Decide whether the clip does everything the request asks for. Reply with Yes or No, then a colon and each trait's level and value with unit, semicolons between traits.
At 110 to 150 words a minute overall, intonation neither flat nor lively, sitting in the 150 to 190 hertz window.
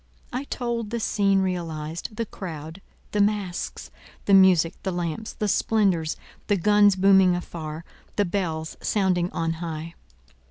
Yes: slow, 135 wpm; average, 3.7 semitones; medium, 185 Hz